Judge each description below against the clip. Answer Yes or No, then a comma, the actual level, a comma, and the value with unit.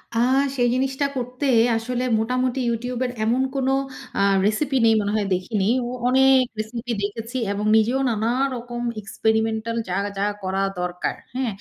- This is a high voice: Yes, high, 230 Hz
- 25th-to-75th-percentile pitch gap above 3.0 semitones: No, narrow, 2.6 semitones